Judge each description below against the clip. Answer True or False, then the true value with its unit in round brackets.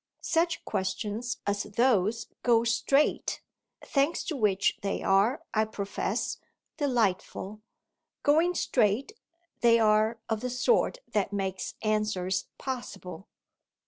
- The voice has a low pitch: False (220 Hz)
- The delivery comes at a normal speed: False (110 wpm)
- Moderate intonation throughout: True (3.9 semitones)